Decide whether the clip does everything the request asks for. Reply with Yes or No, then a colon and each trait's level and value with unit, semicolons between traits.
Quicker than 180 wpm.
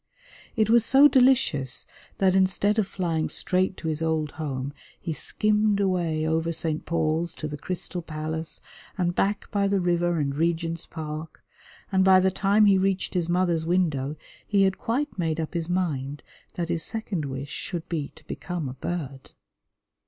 No: average, 170 wpm